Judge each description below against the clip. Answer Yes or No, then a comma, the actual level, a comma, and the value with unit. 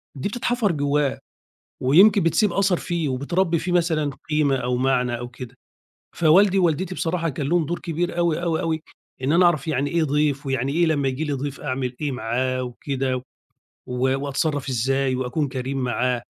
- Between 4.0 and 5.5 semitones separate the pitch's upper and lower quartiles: Yes, average, 4.4 semitones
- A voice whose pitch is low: No, medium, 145 Hz